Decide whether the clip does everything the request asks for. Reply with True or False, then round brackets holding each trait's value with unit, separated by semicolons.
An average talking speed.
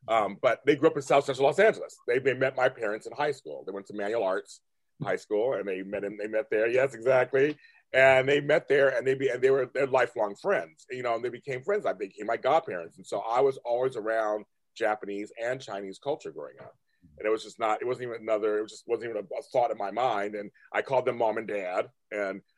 False (260 wpm)